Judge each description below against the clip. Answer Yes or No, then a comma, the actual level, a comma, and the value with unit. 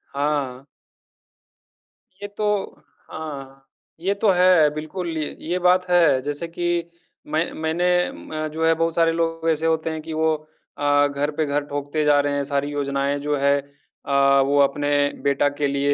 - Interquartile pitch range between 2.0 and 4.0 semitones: Yes, narrow, 2.5 semitones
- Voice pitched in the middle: Yes, medium, 150 Hz